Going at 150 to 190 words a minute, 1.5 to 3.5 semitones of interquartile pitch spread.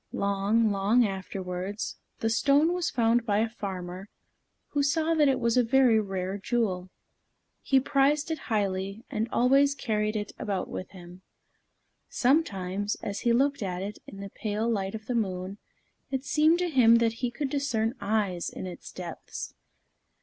No: average, 165 wpm; average, 5.1 semitones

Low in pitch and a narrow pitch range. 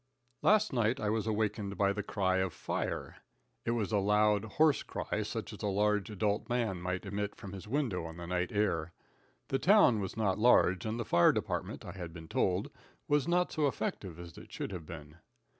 No: low, 105 Hz; average, 3.6 semitones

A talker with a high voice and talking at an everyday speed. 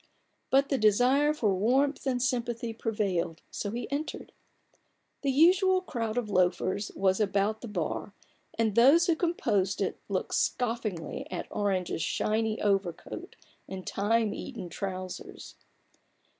No: high, 220 Hz; slow, 130 wpm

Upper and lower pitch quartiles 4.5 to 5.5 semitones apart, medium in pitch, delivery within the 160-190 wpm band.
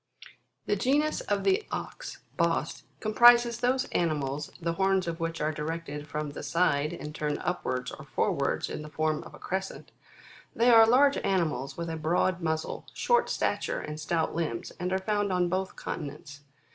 Yes: average, 5.1 semitones; medium, 170 Hz; average, 170 wpm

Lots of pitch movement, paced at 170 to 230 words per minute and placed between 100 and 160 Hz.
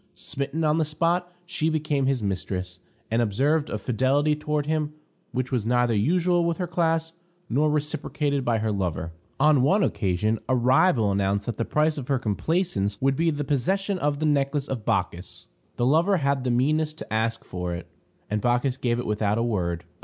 Yes: wide, 5.8 semitones; average, 190 wpm; low, 135 Hz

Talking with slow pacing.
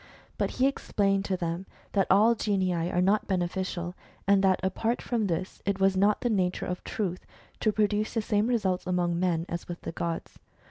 No: average, 195 wpm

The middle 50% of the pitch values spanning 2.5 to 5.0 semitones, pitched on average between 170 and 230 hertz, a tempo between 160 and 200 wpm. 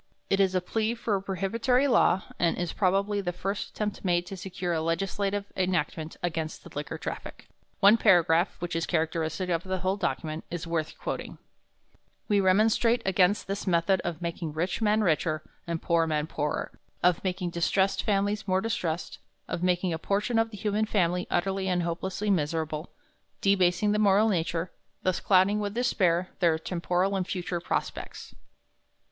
Yes: average, 2.9 semitones; medium, 185 Hz; average, 170 wpm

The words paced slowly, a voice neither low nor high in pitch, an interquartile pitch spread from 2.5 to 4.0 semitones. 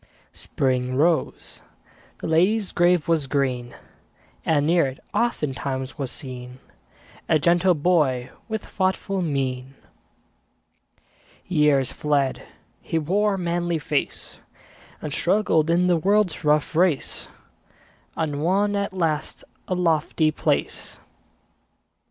No: slow, 110 wpm; medium, 160 Hz; average, 4.4 semitones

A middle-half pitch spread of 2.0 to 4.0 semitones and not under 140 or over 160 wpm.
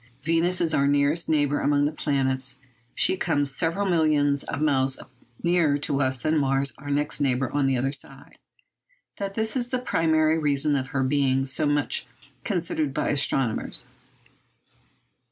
Yes: average, 2.8 semitones; average, 155 wpm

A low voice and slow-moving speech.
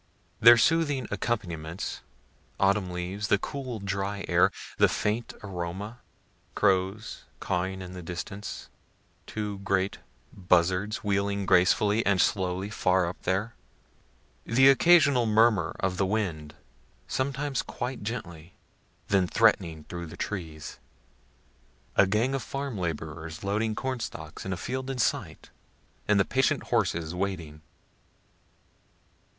Yes: low, 100 Hz; slow, 120 wpm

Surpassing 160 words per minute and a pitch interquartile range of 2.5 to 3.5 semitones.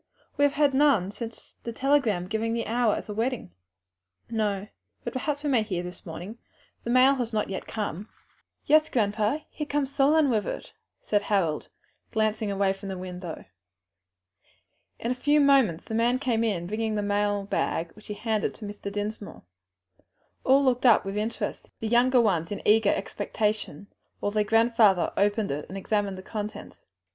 Yes: average, 170 wpm; average, 3.2 semitones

